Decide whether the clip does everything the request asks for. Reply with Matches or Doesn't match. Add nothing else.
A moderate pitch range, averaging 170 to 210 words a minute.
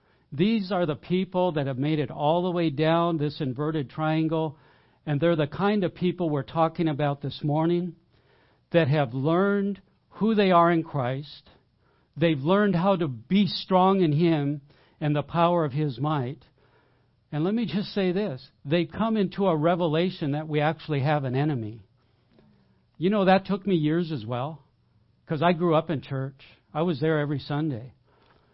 Matches